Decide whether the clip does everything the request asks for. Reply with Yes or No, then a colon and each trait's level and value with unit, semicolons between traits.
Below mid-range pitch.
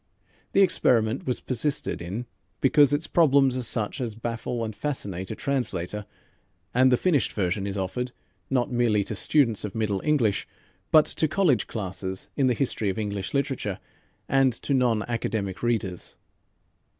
Yes: low, 120 Hz